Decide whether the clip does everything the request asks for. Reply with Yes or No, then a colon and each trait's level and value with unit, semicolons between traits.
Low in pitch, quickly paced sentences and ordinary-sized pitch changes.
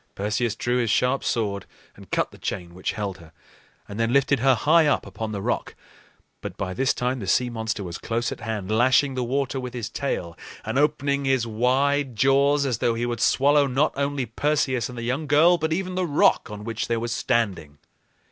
Yes: low, 125 Hz; fast, 210 wpm; average, 4.1 semitones